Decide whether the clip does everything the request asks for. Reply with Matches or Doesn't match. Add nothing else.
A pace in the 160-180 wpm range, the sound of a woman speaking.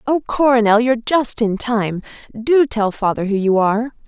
Matches